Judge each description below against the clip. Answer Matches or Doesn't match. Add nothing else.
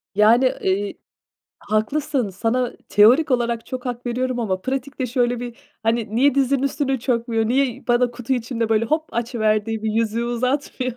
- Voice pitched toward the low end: Doesn't match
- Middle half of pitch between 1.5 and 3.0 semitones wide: Matches